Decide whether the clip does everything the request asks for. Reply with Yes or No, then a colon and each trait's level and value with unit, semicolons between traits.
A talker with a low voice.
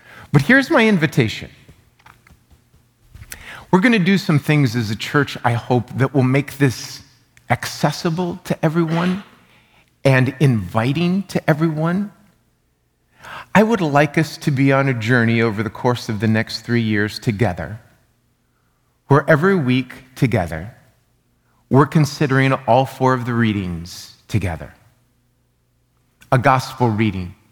Yes: low, 130 Hz